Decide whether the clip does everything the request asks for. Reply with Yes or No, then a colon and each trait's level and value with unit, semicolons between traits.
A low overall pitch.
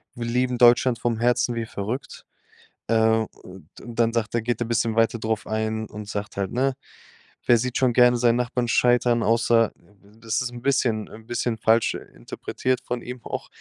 Yes: low, 115 Hz